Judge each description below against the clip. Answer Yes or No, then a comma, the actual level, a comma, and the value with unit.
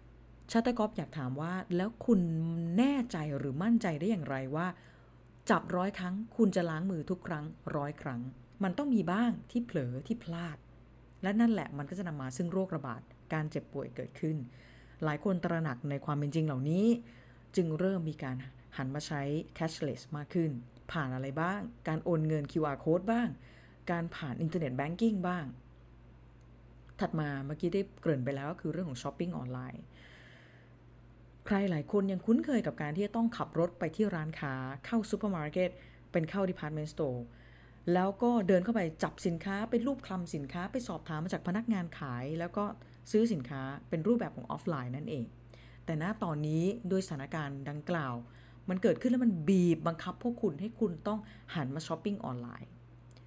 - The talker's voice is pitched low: No, medium, 165 Hz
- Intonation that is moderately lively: No, wide, 5.8 semitones